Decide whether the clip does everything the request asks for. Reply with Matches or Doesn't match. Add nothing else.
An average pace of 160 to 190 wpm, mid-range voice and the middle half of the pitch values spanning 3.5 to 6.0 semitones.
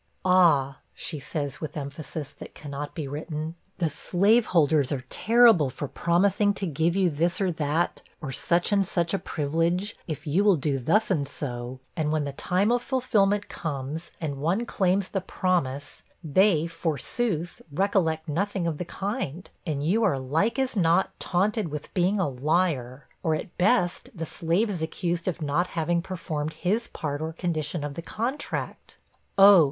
Matches